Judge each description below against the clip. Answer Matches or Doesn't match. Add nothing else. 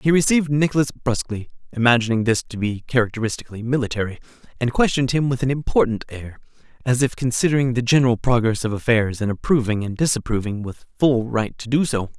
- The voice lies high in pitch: Doesn't match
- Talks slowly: Doesn't match